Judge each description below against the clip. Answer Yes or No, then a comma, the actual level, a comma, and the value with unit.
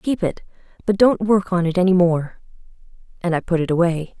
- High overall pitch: No, medium, 180 Hz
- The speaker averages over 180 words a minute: Yes, average, 200 wpm